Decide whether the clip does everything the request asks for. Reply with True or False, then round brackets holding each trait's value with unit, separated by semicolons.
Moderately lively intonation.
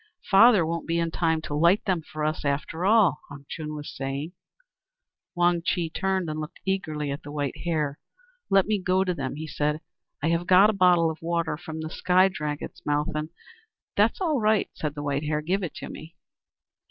True (3.4 semitones)